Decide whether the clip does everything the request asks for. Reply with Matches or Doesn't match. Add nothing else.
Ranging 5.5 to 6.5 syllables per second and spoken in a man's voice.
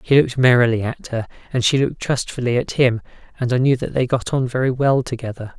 Matches